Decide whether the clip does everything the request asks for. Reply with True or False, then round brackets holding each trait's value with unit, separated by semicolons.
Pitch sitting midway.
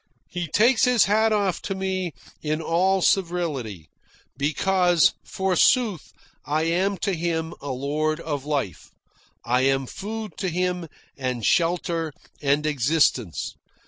True (165 Hz)